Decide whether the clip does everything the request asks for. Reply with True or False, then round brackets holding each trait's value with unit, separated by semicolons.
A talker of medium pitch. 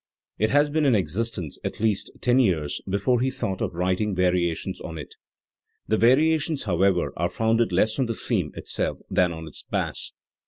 False (105 Hz)